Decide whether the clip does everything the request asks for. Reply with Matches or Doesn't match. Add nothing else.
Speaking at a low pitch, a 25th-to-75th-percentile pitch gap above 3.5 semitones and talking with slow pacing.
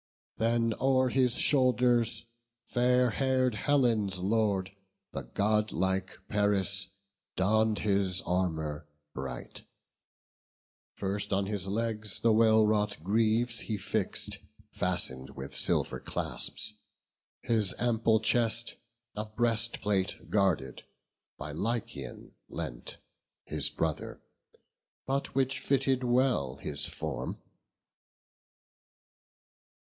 Matches